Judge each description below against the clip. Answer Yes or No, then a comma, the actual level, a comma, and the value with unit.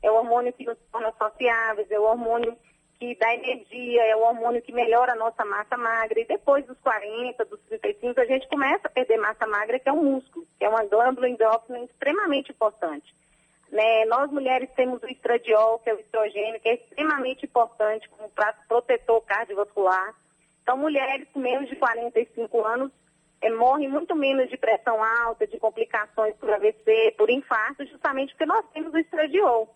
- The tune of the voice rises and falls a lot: No, average, 3.5 semitones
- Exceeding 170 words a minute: Yes, average, 180 wpm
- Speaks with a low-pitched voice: No, high, 235 Hz